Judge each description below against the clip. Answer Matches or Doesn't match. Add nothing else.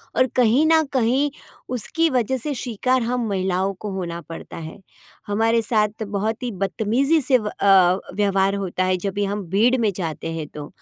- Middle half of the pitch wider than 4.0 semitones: Matches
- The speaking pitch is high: Matches